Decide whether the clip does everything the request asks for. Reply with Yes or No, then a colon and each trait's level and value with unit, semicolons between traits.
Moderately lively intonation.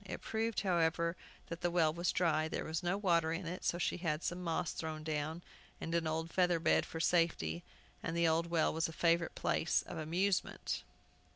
No: narrow, 1.6 semitones